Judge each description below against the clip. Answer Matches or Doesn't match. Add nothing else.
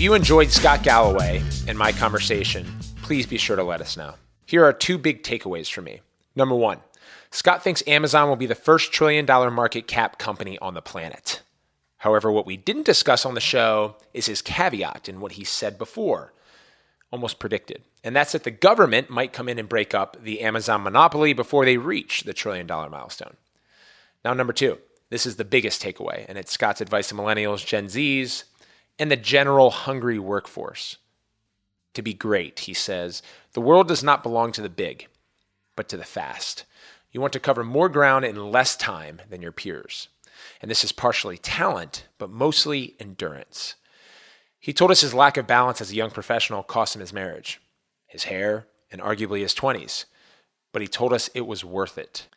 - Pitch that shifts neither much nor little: Matches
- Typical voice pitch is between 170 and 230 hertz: Doesn't match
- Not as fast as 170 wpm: Doesn't match